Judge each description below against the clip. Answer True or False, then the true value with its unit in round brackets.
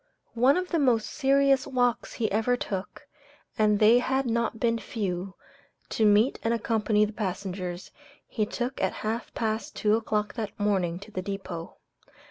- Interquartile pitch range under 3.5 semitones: True (3.0 semitones)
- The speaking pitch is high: True (220 Hz)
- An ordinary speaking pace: True (160 wpm)